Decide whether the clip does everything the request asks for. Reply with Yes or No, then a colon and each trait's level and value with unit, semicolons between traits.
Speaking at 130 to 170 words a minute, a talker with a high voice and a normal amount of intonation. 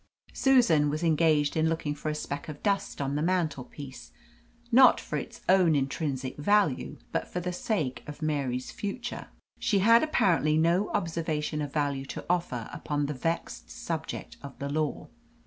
No: average, 165 wpm; medium, 155 Hz; average, 3.8 semitones